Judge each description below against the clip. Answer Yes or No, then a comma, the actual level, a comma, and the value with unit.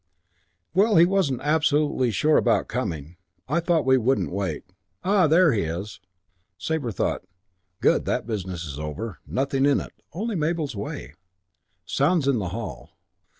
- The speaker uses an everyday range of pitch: No, wide, 8.1 semitones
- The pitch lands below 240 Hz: Yes, low, 135 Hz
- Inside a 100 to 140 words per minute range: No, average, 150 wpm